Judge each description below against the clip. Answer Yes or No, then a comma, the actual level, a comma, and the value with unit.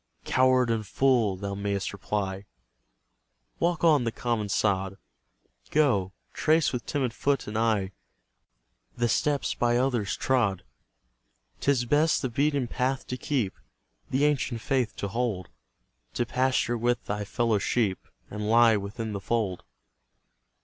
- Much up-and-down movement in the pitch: No, average, 4.3 semitones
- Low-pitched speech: Yes, low, 120 Hz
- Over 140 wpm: No, slow, 135 wpm